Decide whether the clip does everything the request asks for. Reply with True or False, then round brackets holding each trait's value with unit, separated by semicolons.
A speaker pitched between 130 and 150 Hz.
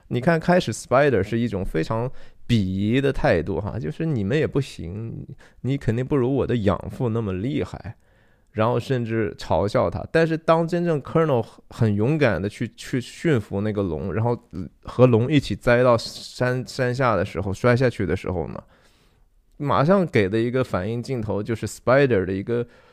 False (115 Hz)